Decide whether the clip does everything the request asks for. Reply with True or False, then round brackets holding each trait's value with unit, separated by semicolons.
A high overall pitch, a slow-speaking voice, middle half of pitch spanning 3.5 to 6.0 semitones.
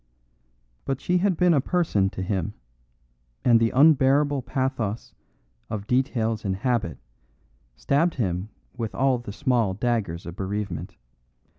False (120 Hz; 130 wpm; 5.1 semitones)